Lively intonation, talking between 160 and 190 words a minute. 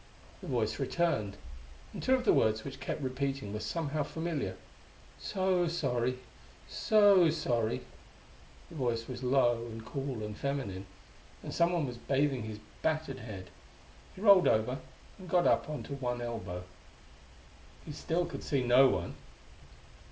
No: wide, 5.8 semitones; average, 145 wpm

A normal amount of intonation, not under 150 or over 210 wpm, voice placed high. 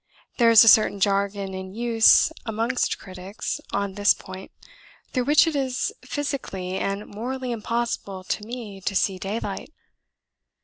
No: average, 3.6 semitones; average, 140 wpm; high, 210 Hz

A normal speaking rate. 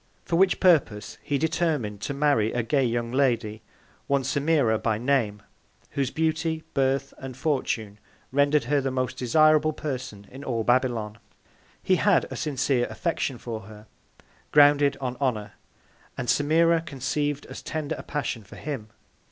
Yes: average, 150 wpm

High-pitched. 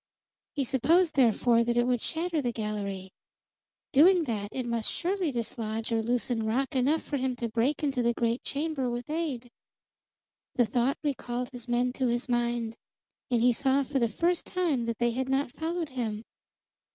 Yes: high, 245 Hz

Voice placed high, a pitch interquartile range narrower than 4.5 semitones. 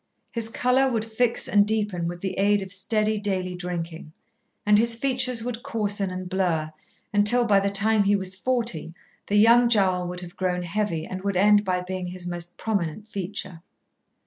Yes: high, 200 Hz; average, 3.3 semitones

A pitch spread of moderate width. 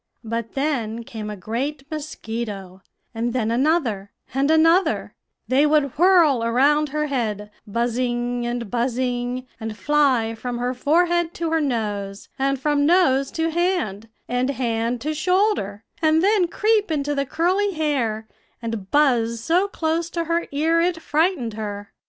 No: wide, 5.7 semitones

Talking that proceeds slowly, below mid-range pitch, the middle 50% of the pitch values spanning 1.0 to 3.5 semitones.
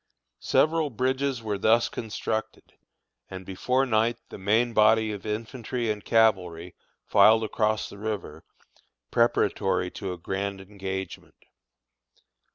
Yes: slow, 115 wpm; low, 110 Hz; average, 3.2 semitones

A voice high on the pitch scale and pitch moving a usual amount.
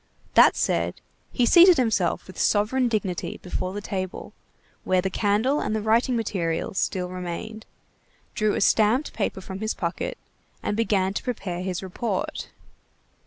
Yes: high, 205 Hz; average, 3.5 semitones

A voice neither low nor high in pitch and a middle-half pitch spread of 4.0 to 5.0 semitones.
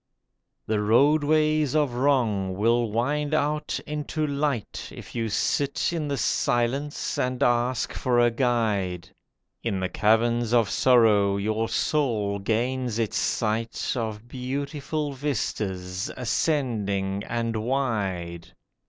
No: low, 120 Hz; average, 4.7 semitones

